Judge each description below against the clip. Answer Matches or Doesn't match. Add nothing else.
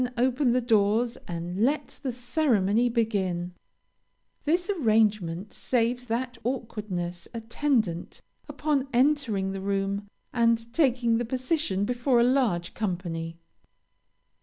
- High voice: Matches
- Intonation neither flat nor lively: Matches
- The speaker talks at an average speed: Doesn't match